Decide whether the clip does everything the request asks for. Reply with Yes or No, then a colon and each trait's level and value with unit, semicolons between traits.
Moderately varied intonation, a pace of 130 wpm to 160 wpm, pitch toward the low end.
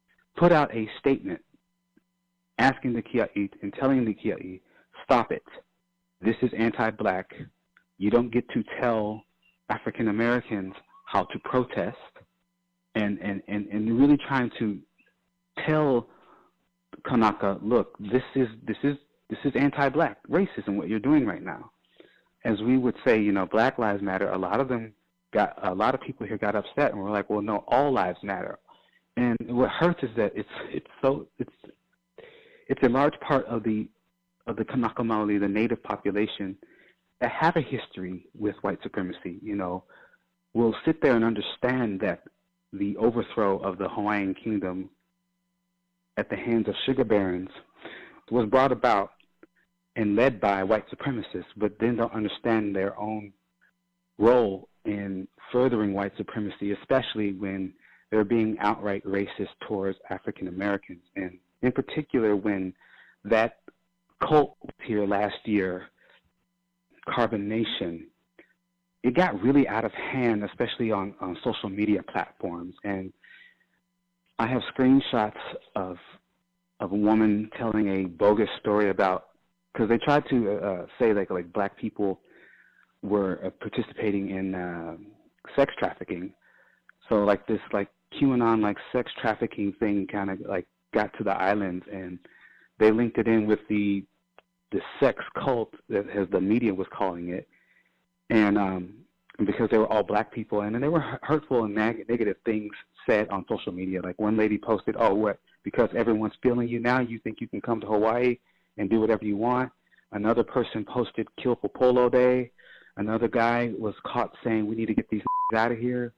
Yes: average, 3.6 semitones; average, 155 wpm; low, 105 Hz